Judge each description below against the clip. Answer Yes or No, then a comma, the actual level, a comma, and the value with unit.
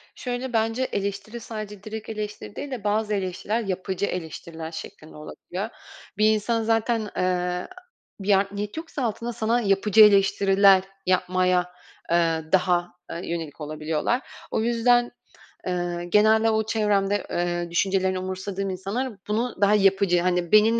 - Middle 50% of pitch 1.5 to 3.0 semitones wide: No, average, 3.4 semitones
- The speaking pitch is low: No, high, 200 Hz